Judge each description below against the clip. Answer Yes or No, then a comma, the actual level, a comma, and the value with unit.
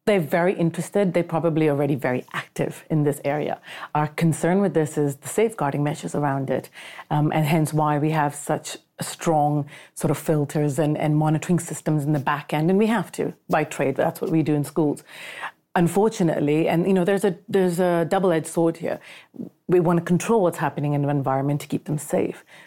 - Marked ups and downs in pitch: No, average, 2.8 semitones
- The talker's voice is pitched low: No, medium, 155 Hz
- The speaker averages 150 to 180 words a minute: No, fast, 205 wpm